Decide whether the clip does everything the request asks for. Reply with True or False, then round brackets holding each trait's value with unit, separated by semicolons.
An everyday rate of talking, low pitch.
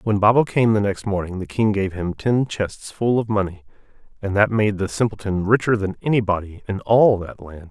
False (210 wpm; 100 Hz)